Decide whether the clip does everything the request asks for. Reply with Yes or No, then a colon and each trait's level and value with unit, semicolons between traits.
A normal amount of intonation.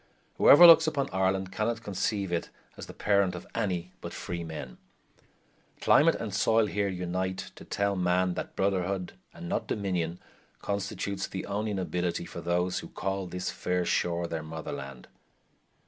No: narrow, 2.3 semitones